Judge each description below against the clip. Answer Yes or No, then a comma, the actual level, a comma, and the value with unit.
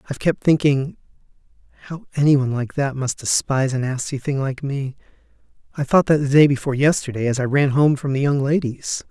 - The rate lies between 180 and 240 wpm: Yes, average, 200 wpm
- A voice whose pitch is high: No, medium, 140 Hz